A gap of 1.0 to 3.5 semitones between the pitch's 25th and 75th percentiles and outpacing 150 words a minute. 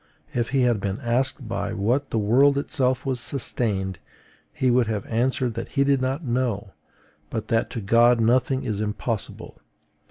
Yes: average, 2.9 semitones; average, 165 wpm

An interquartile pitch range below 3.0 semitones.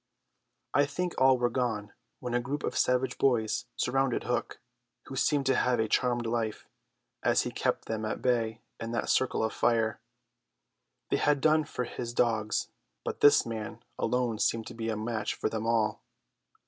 Yes: narrow, 2.5 semitones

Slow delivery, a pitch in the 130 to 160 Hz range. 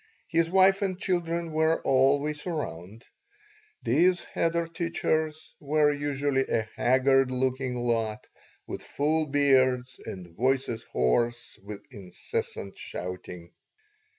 Yes: slow, 105 wpm; low, 135 Hz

